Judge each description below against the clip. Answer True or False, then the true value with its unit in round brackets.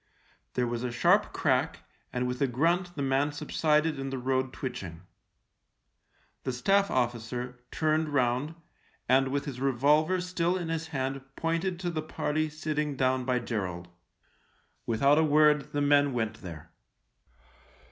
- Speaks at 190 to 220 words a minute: False (150 wpm)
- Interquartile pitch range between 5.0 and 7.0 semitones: False (3.8 semitones)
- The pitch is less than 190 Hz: True (140 Hz)